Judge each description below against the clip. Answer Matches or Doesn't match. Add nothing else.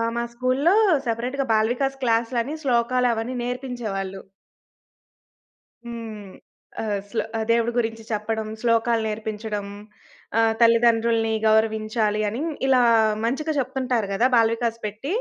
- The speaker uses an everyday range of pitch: Doesn't match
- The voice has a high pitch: Matches